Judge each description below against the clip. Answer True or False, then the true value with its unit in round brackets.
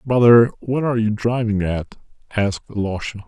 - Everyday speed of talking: True (145 wpm)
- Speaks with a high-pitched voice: False (110 Hz)